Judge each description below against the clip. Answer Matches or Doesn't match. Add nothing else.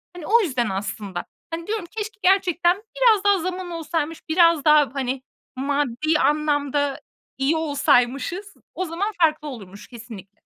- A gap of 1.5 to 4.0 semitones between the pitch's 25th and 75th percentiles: Doesn't match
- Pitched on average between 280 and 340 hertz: Matches